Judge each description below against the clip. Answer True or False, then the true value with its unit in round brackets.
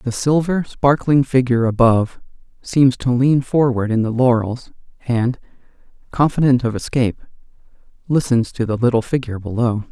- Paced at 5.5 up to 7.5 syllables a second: False (5.1 syllables/s)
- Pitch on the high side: False (125 Hz)